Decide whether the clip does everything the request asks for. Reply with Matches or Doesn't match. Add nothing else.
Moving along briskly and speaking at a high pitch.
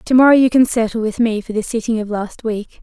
Matches